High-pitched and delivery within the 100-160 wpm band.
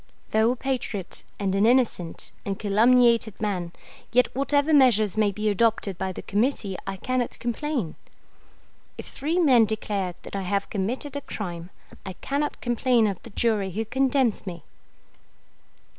Yes: high, 220 Hz; average, 150 wpm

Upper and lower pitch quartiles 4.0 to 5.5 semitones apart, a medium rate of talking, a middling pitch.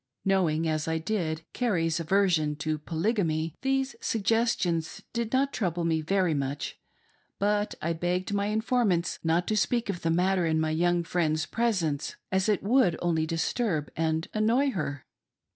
Yes: average, 4.8 semitones; average, 155 wpm; medium, 175 Hz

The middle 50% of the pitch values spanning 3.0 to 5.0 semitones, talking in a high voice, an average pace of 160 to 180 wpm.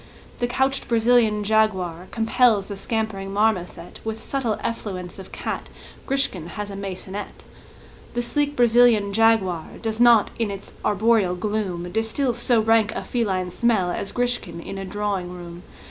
No: average, 3.5 semitones; high, 215 Hz; average, 145 wpm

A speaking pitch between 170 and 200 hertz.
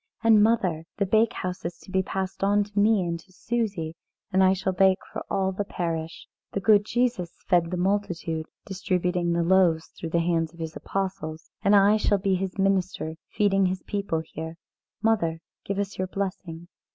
Yes: high, 190 Hz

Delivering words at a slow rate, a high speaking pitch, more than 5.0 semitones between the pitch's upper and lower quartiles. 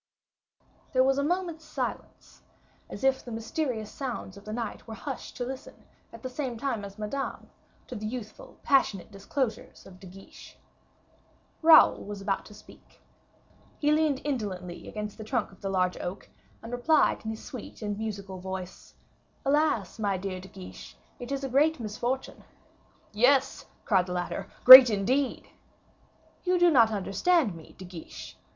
No: average, 160 wpm; high, 220 Hz; wide, 5.4 semitones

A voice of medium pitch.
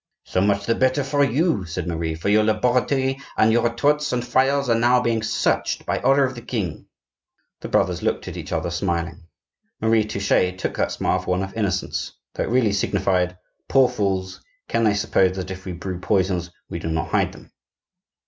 No: low, 105 Hz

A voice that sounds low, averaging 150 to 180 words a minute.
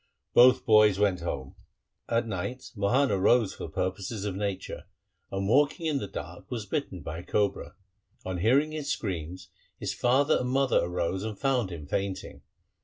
Yes: low, 105 Hz; average, 165 wpm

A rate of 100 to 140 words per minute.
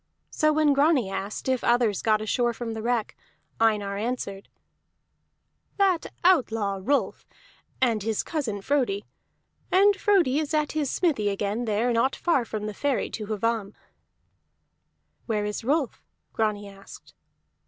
Yes: slow, 135 wpm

